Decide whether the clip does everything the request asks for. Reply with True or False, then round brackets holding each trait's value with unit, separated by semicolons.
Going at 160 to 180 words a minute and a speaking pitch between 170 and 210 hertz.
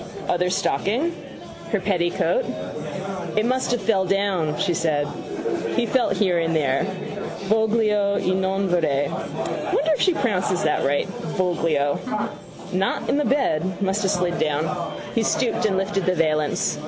False (145 wpm; 190 Hz)